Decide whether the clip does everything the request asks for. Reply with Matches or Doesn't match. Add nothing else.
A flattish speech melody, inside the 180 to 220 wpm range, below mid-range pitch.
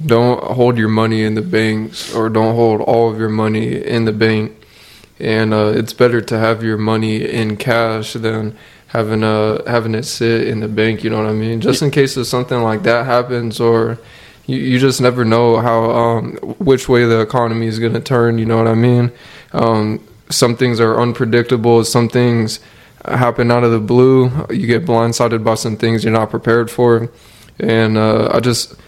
Matches